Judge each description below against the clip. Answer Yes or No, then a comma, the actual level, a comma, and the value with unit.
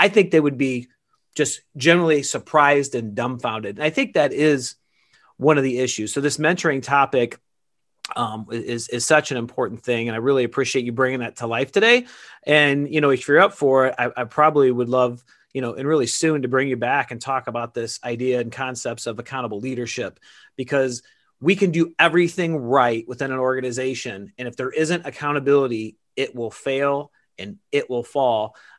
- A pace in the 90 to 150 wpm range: No, average, 195 wpm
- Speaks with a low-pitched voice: Yes, low, 130 Hz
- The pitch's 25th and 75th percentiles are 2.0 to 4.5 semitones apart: Yes, average, 3.3 semitones